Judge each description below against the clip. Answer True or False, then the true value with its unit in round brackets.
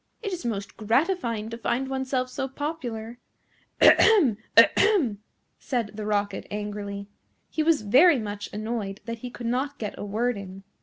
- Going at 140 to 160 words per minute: True (155 wpm)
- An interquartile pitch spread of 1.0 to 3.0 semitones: False (4.4 semitones)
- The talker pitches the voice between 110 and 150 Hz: False (230 Hz)